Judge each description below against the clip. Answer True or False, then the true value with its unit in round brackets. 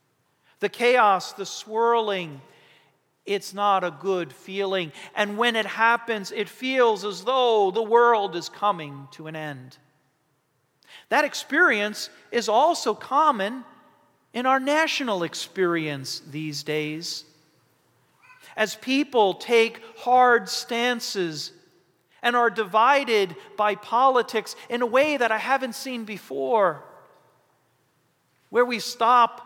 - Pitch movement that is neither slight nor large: False (6.1 semitones)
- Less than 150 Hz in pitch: False (215 Hz)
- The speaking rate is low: True (115 wpm)